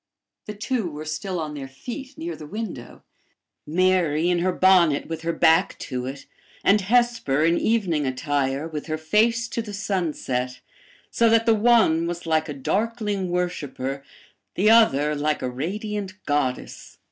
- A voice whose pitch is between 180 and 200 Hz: No, medium, 170 Hz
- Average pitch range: No, wide, 6.1 semitones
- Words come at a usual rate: Yes, average, 160 wpm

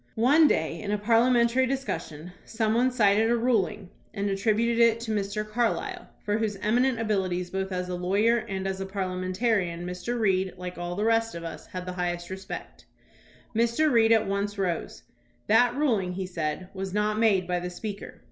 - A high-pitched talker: Yes, high, 205 Hz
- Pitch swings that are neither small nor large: Yes, average, 3.8 semitones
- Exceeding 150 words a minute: Yes, average, 185 wpm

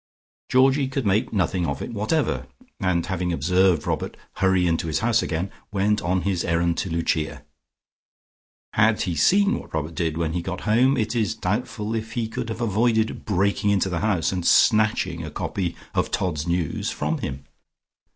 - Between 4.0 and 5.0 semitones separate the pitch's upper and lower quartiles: Yes, average, 4.5 semitones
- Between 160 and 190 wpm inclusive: Yes, average, 175 wpm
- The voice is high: No, very low, 95 Hz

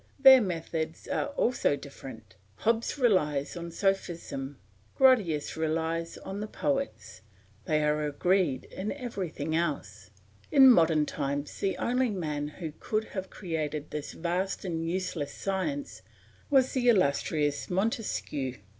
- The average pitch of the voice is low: No, medium, 170 Hz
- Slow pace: Yes, slow, 125 wpm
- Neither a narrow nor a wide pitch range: No, wide, 6.1 semitones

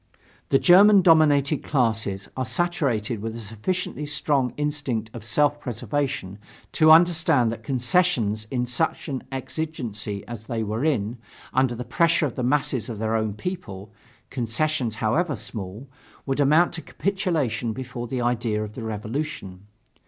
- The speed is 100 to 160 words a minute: Yes, average, 145 wpm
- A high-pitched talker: No, low, 125 Hz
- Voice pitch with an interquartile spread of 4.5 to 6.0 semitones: Yes, average, 5.2 semitones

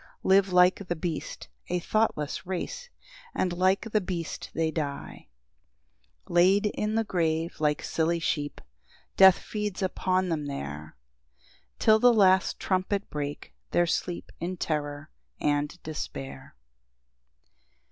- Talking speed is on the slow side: Yes, slow, 125 wpm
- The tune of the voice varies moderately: Yes, average, 4.1 semitones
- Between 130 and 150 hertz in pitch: No, medium, 175 Hz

